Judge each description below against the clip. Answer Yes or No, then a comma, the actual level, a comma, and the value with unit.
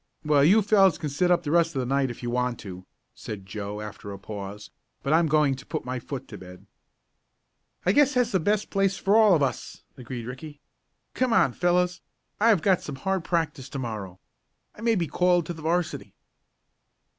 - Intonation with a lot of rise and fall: Yes, wide, 6.7 semitones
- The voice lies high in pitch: No, medium, 150 Hz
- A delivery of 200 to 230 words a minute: Yes, fast, 205 wpm